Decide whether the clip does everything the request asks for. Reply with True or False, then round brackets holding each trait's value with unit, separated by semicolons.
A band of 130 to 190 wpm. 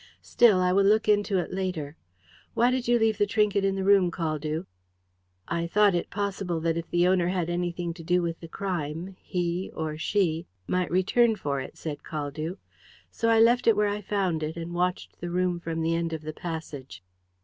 False (205 wpm)